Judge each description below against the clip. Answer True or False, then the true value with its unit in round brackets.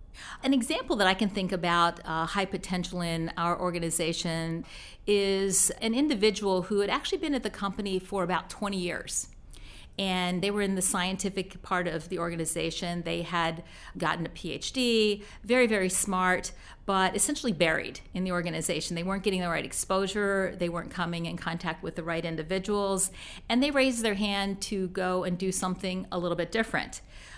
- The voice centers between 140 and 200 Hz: True (185 Hz)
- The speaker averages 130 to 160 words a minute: False (175 wpm)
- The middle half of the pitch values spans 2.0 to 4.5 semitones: True (2.8 semitones)